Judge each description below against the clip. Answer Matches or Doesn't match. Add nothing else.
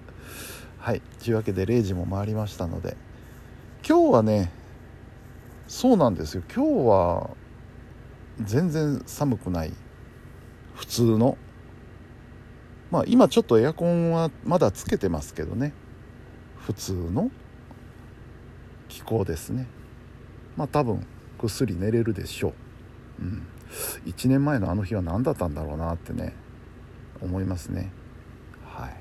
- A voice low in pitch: Matches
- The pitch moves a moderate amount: Matches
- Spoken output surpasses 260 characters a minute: Doesn't match